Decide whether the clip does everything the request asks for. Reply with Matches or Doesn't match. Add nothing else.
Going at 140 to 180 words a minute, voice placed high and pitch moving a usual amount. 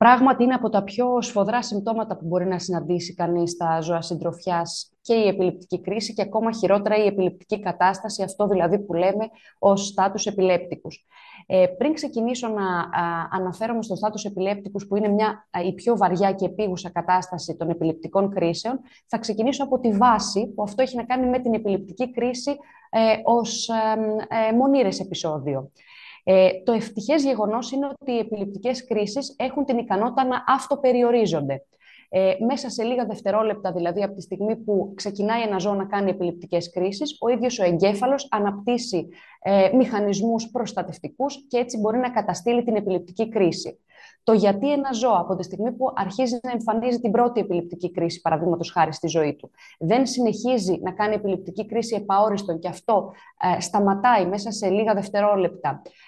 Matches